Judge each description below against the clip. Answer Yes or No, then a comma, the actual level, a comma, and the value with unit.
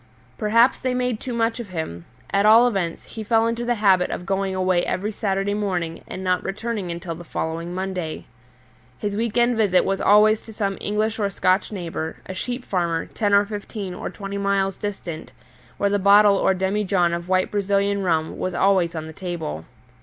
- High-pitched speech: Yes, high, 195 Hz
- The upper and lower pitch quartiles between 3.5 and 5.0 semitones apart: No, average, 2.8 semitones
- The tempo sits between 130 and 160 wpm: No, average, 195 wpm